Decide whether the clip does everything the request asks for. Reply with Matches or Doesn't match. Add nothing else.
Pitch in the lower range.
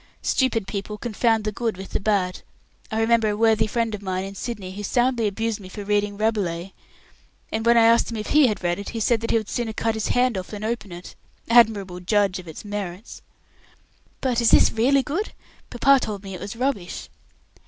Doesn't match